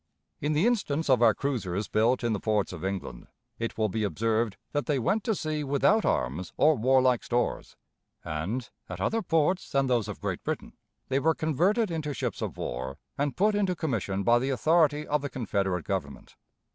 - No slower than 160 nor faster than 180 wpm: No, average, 190 wpm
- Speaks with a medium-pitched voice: No, low, 130 Hz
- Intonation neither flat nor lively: No, wide, 6.6 semitones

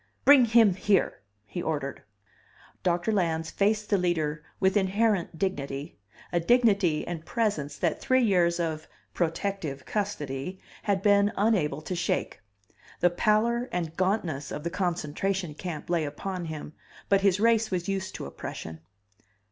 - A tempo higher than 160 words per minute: No, average, 140 wpm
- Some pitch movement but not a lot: Yes, average, 4.2 semitones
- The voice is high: No, medium, 180 Hz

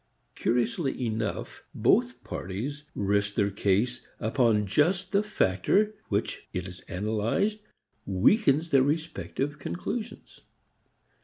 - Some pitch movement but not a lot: No, wide, 8.0 semitones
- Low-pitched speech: Yes, low, 125 Hz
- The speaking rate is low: Yes, slow, 105 wpm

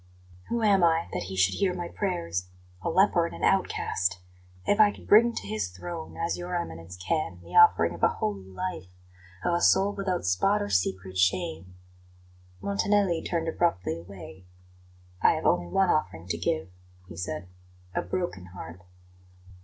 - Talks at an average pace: Yes, average, 170 wpm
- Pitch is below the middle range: Yes, low, 100 Hz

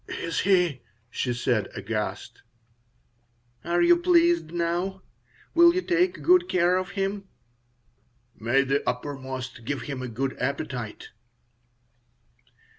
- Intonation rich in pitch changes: Yes, wide, 7.6 semitones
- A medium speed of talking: No, slow, 115 wpm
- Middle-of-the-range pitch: Yes, medium, 165 Hz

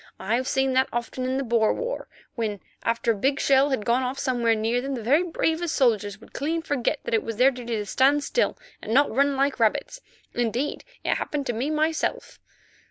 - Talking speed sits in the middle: No, fast, 210 wpm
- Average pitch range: Yes, average, 3.5 semitones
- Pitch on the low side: No, very high, 255 Hz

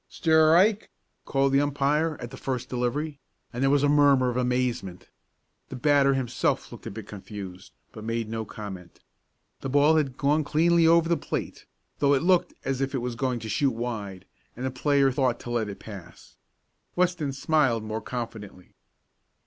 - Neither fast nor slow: Yes, average, 180 wpm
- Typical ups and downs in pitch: Yes, average, 4.1 semitones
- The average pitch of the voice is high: No, low, 130 Hz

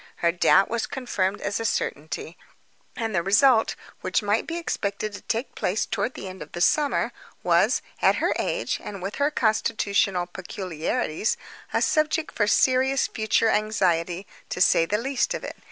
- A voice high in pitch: Yes, high, 210 Hz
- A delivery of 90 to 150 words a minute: No, average, 170 wpm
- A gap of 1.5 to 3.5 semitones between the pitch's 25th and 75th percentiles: No, average, 4.7 semitones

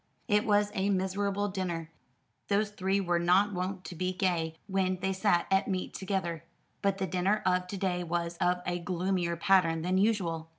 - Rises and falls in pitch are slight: Yes, narrow, 1.9 semitones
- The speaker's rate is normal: Yes, average, 180 wpm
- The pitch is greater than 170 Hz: Yes, medium, 185 Hz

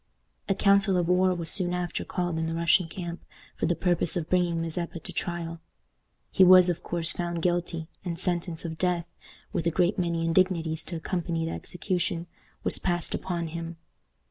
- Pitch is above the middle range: No, medium, 175 Hz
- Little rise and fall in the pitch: Yes, narrow, 1.4 semitones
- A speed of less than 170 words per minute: No, average, 180 wpm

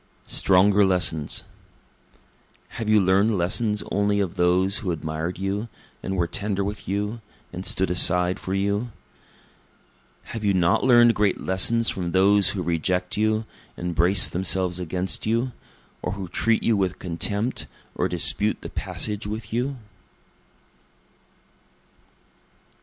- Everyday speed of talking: No, slow, 130 wpm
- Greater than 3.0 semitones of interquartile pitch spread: No, average, 2.7 semitones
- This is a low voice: Yes, very low, 95 Hz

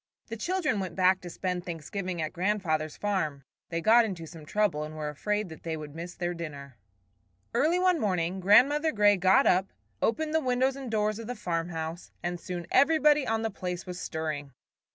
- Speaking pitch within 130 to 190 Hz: Yes, medium, 185 Hz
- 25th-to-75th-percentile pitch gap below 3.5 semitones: No, average, 5.2 semitones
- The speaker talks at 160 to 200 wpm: Yes, average, 190 wpm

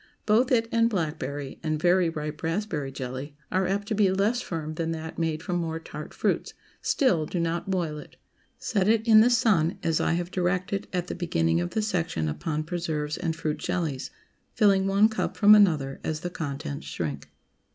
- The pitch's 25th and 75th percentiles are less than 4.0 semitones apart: No, average, 4.3 semitones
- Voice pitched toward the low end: No, medium, 170 Hz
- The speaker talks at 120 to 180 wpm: No, average, 190 wpm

